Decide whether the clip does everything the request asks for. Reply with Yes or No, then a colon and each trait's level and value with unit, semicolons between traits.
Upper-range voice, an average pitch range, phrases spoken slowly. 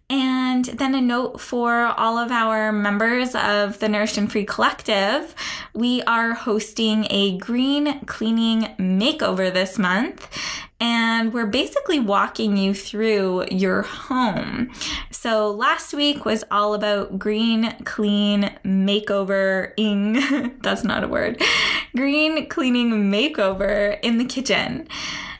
Yes: high, 225 Hz; average, 3.4 semitones; slow, 125 wpm